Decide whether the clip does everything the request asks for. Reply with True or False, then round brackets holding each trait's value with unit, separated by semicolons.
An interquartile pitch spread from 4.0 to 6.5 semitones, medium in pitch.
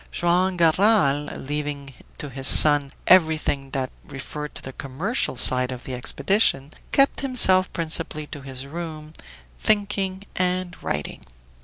True (5.1 semitones; 155 Hz)